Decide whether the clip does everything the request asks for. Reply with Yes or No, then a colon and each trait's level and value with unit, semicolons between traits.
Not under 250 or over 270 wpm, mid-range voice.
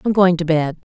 Yes: fast, 260 wpm; medium, 175 Hz